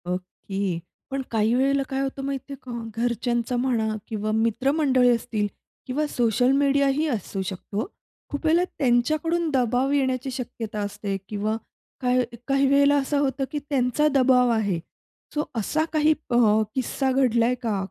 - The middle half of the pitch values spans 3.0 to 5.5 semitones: Yes, average, 3.7 semitones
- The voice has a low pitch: No, very high, 255 Hz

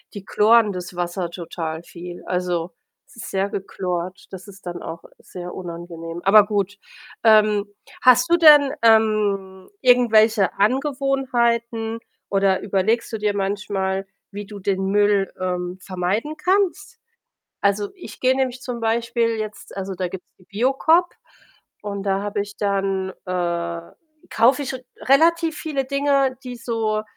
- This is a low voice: No, high, 205 Hz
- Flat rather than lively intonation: No, average, 4.1 semitones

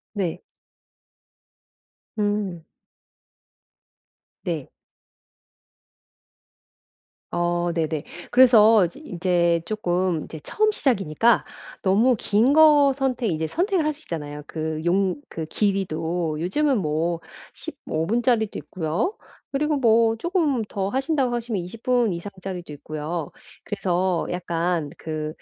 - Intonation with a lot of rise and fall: Yes, wide, 6.4 semitones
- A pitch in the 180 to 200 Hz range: Yes, high, 190 Hz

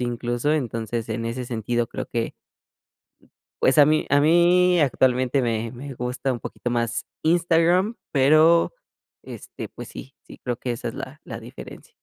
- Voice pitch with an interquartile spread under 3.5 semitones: No, average, 4.7 semitones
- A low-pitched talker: Yes, low, 130 Hz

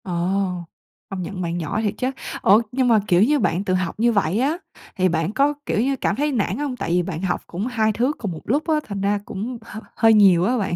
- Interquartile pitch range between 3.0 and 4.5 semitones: No, average, 5.1 semitones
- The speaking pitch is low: No, high, 205 Hz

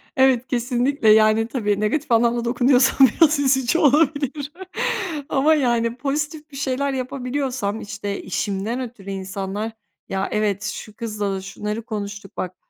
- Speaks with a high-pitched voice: Yes, high, 240 Hz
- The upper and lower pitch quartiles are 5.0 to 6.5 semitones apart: No, average, 4.5 semitones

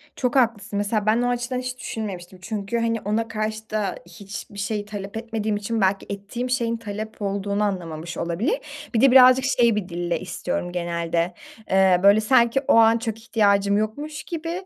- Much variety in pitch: No, average, 3.0 semitones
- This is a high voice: Yes, high, 215 Hz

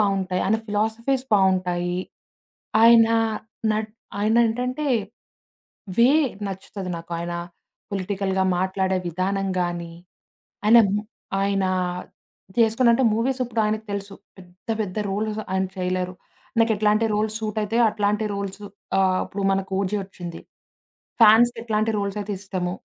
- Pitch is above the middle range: Yes, high, 200 Hz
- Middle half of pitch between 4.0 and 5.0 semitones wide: No, average, 2.7 semitones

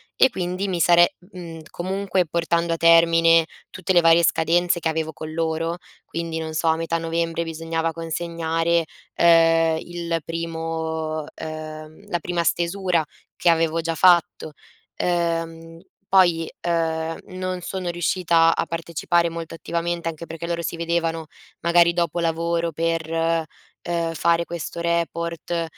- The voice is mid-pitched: Yes, medium, 165 Hz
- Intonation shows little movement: Yes, narrow, 0.8 semitones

